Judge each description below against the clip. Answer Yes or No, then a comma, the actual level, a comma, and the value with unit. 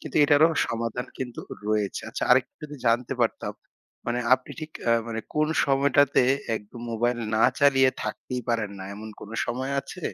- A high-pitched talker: No, low, 125 Hz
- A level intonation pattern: No, average, 3.5 semitones